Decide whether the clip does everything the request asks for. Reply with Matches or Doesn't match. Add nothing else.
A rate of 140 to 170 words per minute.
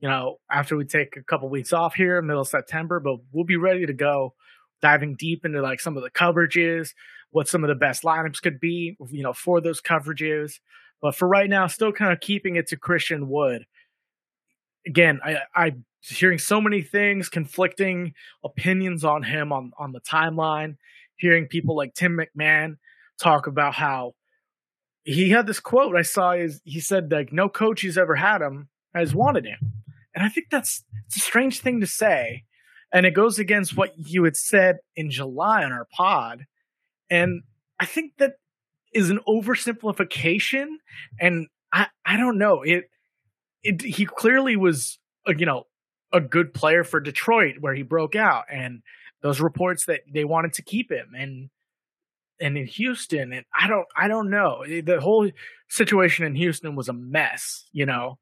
Doesn't match